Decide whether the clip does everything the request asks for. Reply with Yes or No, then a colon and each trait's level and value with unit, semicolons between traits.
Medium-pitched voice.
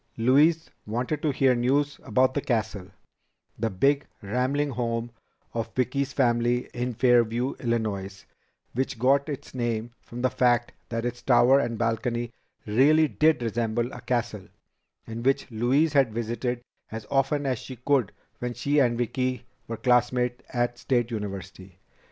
No: low, 120 Hz